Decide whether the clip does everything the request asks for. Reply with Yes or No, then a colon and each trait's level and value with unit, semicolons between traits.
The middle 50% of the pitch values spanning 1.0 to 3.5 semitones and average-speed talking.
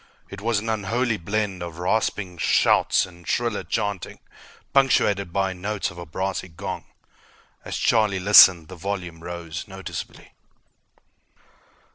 No: average, 3.0 semitones; slow, 125 wpm